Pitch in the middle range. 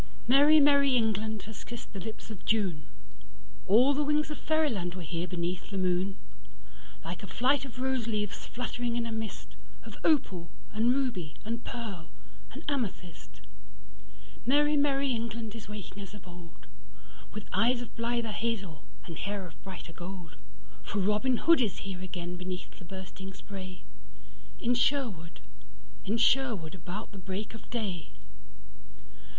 No: high, 205 Hz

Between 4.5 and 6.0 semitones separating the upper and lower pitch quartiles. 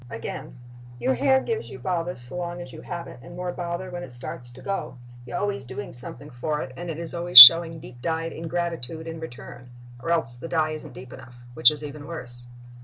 Yes: wide, 5.4 semitones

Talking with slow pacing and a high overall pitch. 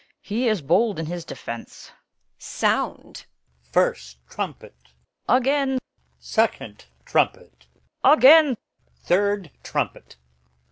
Yes: slow, 100 wpm; high, 205 Hz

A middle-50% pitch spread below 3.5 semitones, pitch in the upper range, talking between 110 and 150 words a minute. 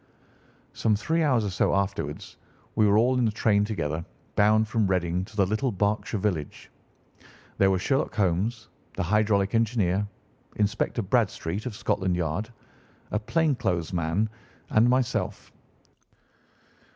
No: average, 3.1 semitones; low, 105 Hz; average, 140 wpm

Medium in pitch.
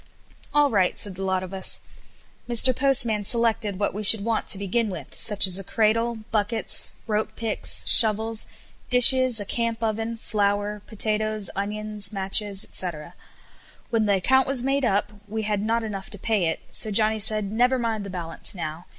No: high, 215 Hz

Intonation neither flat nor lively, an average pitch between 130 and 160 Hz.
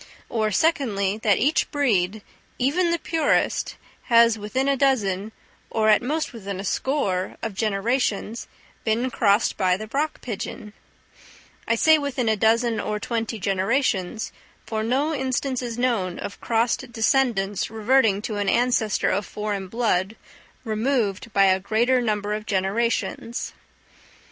No: average, 3.8 semitones; high, 225 Hz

